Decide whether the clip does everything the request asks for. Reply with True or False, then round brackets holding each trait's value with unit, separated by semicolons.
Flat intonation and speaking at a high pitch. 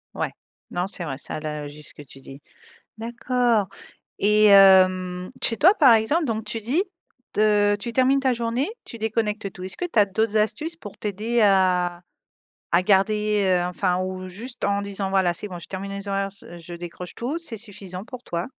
False (3.7 semitones; 205 Hz)